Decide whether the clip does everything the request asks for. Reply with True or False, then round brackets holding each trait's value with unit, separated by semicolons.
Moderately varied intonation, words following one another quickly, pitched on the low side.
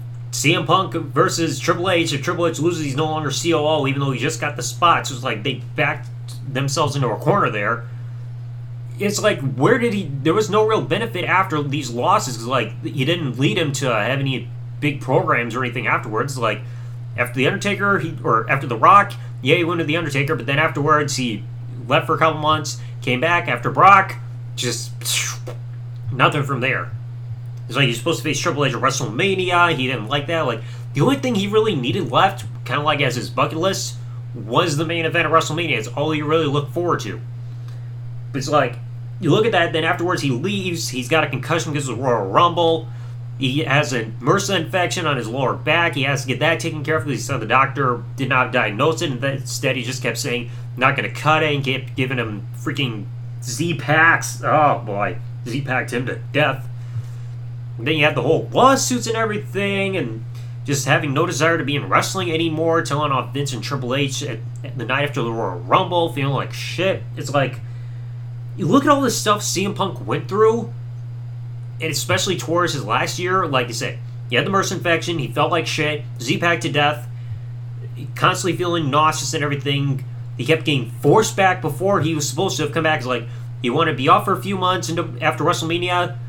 True (4.5 semitones; 210 wpm; 130 Hz)